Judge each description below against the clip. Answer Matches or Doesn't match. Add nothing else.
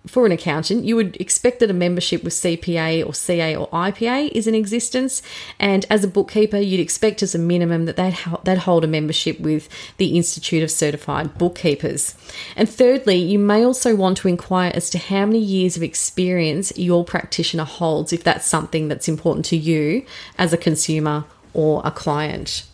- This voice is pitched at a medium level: Matches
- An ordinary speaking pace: Matches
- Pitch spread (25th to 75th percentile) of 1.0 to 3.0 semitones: Doesn't match